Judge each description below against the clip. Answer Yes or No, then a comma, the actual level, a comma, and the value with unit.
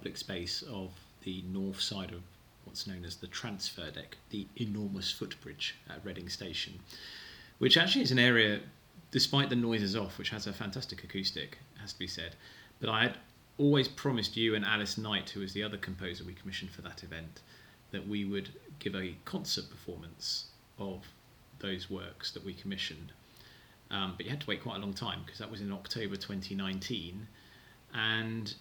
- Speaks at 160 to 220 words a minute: Yes, average, 180 wpm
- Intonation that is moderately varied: Yes, average, 3.4 semitones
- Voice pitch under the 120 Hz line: Yes, low, 100 Hz